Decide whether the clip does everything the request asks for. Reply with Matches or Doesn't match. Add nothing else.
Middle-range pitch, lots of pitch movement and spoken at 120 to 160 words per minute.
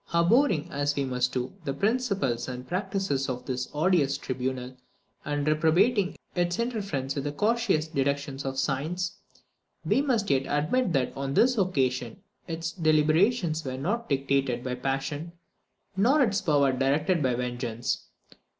Matches